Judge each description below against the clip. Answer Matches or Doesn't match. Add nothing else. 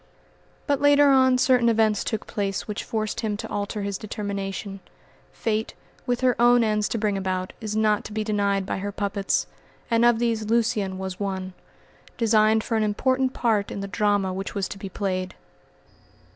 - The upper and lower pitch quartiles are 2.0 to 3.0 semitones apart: Matches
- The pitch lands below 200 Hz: Doesn't match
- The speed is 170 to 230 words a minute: Matches